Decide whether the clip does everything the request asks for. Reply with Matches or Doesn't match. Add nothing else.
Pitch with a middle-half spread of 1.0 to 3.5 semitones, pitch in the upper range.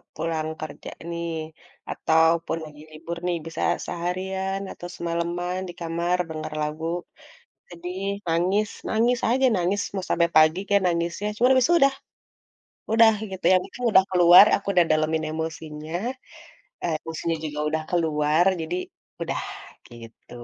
Doesn't match